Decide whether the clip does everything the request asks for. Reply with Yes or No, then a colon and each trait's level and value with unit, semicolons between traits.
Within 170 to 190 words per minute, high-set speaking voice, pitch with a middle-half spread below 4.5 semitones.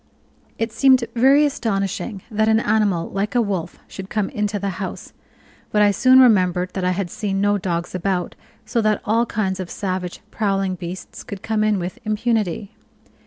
Yes: average, 175 wpm; high, 205 Hz; average, 2.8 semitones